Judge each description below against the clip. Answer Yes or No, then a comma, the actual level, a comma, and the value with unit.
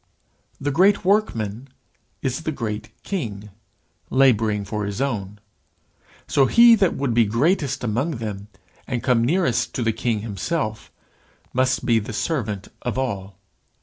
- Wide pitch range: No, average, 4.7 semitones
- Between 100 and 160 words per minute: Yes, average, 140 wpm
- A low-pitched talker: Yes, low, 120 Hz